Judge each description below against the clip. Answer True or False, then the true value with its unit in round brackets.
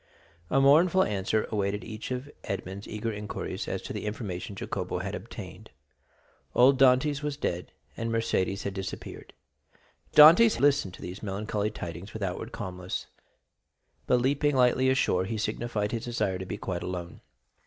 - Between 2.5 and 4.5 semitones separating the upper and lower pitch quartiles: False (5.2 semitones)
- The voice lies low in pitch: True (110 Hz)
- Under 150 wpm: False (155 wpm)